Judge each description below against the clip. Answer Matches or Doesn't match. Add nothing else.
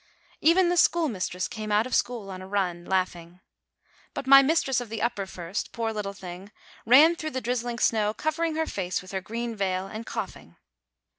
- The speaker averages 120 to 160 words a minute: Doesn't match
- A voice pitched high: Matches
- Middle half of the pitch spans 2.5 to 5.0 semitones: Doesn't match